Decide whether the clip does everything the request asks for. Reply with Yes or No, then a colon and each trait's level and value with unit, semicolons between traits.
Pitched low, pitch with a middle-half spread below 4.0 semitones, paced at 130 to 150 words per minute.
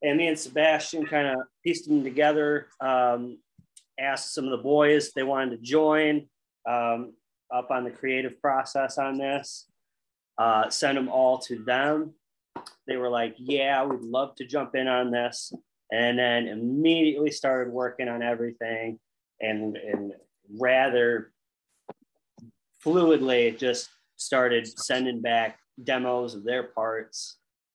Yes: low, 130 Hz; average, 3.4 semitones; average, 140 wpm